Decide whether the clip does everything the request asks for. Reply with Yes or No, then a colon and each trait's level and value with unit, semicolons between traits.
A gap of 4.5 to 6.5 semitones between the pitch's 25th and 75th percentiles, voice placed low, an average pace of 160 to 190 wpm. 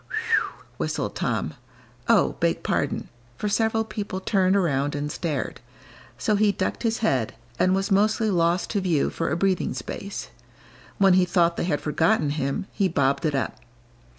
No: average, 5.2 semitones; medium, 185 Hz; average, 165 wpm